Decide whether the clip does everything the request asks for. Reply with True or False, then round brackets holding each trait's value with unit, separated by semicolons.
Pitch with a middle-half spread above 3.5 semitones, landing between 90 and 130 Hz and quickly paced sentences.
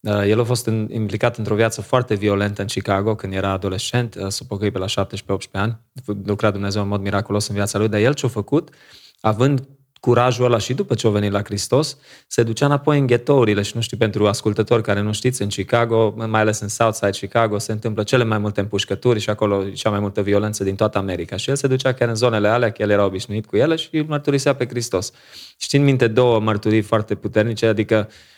False (3.0 semitones; 110 Hz; 220 wpm)